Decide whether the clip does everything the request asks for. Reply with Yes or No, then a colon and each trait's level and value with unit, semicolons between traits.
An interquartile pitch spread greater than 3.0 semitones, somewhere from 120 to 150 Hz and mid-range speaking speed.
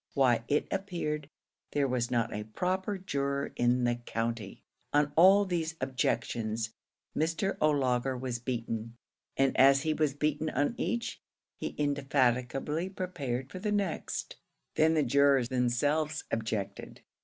No: average, 4.5 semitones; medium, 140 Hz; slow, 130 wpm